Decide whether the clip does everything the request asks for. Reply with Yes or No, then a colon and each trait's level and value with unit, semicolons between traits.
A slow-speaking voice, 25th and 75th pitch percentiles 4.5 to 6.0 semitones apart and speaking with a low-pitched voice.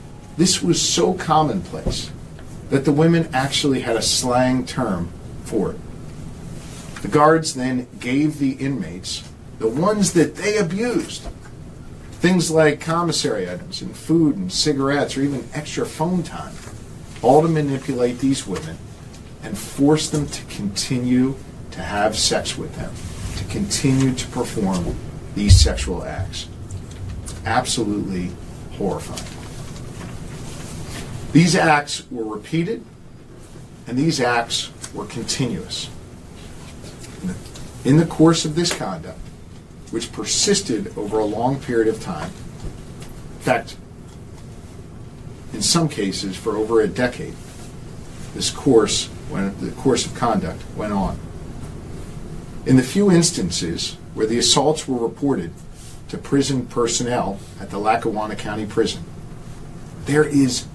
Yes: slow, 120 wpm; wide, 5.6 semitones; low, 130 Hz